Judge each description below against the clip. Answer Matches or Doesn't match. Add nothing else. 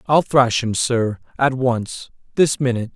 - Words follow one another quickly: Doesn't match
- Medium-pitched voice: Doesn't match